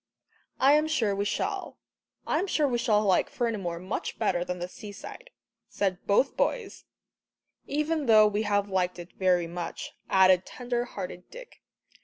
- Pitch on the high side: Yes, high, 205 Hz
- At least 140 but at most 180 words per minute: Yes, average, 160 wpm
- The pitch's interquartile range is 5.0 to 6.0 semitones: Yes, average, 5.3 semitones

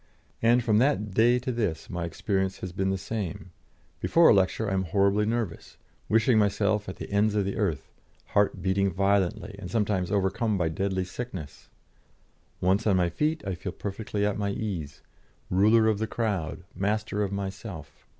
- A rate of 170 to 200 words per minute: Yes, average, 175 wpm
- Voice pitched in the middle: No, low, 100 Hz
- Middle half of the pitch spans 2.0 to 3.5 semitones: Yes, narrow, 2.5 semitones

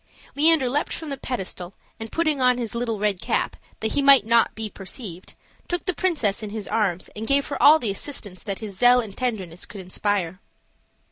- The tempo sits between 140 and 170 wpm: No, average, 200 wpm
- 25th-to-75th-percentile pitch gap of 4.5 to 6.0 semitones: Yes, wide, 5.6 semitones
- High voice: Yes, high, 225 Hz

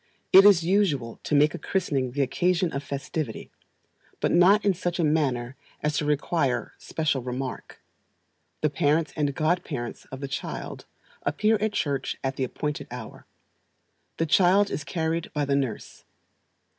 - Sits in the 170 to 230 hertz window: No, medium, 150 Hz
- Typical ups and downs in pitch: Yes, average, 4.4 semitones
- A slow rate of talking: No, average, 155 wpm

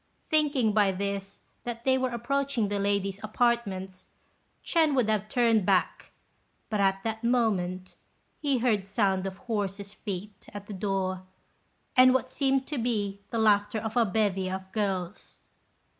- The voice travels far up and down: No, average, 3.6 semitones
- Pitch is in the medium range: No, high, 210 Hz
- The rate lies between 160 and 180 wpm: No, average, 150 wpm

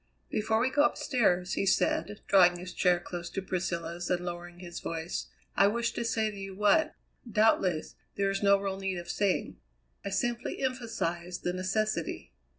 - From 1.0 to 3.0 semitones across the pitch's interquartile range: No, average, 3.5 semitones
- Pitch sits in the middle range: No, high, 195 Hz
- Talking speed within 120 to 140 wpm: No, average, 170 wpm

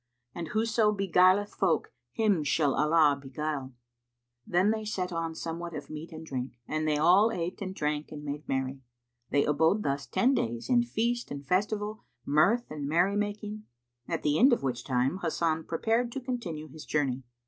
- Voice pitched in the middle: Yes, medium, 165 Hz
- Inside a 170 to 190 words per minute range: Yes, average, 175 wpm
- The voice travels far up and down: Yes, wide, 6.0 semitones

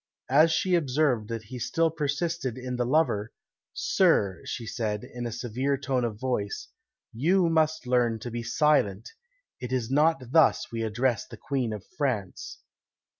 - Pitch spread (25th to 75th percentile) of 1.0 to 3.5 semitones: No, average, 4.8 semitones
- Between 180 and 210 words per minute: No, average, 160 wpm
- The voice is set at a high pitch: No, low, 125 Hz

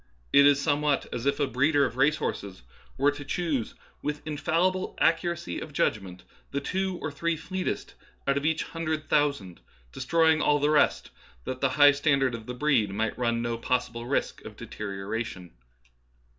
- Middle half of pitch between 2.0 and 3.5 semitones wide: No, average, 4.7 semitones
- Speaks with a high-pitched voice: No, medium, 140 Hz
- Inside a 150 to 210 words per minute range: Yes, average, 170 wpm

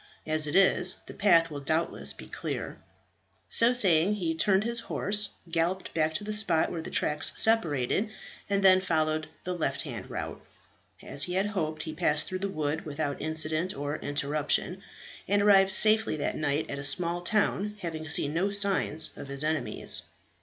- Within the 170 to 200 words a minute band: Yes, average, 175 wpm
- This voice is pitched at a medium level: Yes, medium, 165 Hz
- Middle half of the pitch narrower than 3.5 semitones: No, average, 4.2 semitones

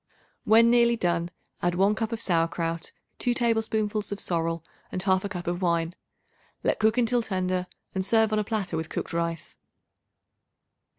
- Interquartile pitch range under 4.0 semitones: No, average, 4.5 semitones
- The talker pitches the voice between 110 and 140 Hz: No, high, 190 Hz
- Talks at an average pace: Yes, average, 160 wpm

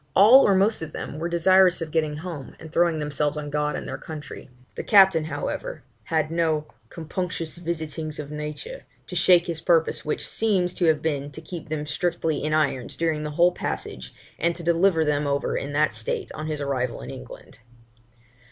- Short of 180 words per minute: No, average, 190 wpm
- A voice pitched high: No, medium, 160 Hz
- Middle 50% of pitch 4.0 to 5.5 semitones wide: No, narrow, 2.5 semitones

